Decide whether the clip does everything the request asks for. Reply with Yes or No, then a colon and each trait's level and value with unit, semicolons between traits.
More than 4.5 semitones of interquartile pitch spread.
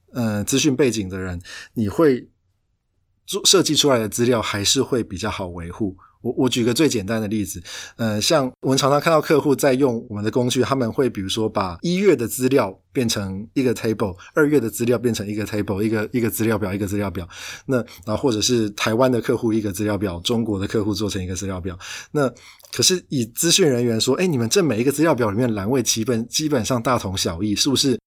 No: average, 3.8 semitones